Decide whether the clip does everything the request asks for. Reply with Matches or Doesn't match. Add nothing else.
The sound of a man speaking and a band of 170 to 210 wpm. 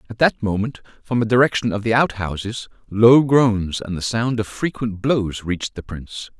Matches